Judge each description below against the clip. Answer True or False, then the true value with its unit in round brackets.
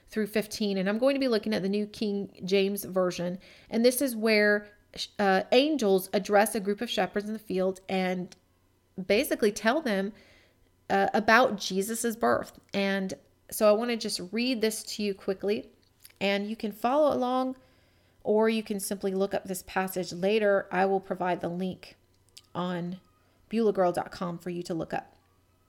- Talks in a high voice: True (200 Hz)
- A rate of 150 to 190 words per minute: True (170 wpm)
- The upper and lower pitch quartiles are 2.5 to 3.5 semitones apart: True (2.8 semitones)